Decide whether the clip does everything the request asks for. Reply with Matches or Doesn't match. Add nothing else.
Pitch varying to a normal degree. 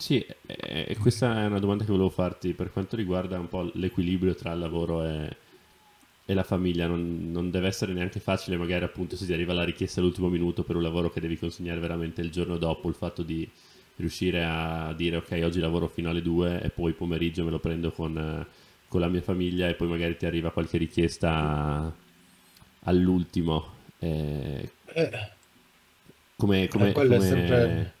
Doesn't match